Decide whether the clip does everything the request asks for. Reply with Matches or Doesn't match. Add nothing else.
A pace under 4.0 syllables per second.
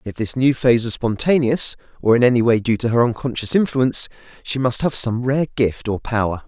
Doesn't match